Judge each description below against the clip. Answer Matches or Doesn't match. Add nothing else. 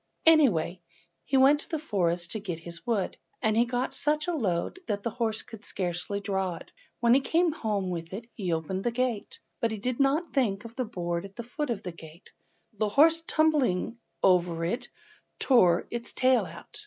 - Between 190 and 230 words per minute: Matches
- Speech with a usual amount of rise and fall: Doesn't match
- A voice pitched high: Matches